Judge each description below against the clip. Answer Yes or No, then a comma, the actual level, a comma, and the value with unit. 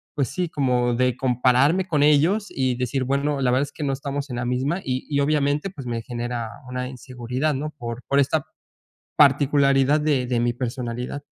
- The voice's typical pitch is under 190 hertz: Yes, low, 135 Hz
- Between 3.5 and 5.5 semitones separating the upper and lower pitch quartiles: No, average, 2.7 semitones